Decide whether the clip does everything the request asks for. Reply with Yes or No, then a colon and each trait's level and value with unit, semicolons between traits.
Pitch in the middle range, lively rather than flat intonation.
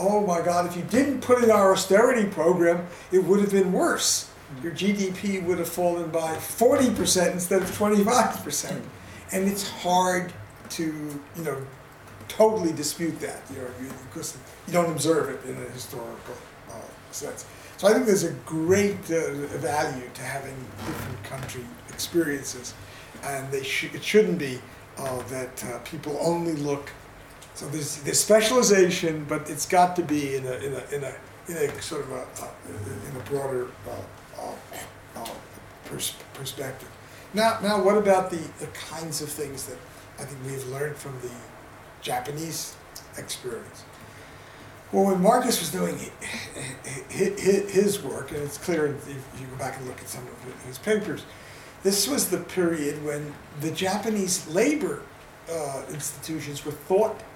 Yes: medium, 155 Hz; wide, 5.9 semitones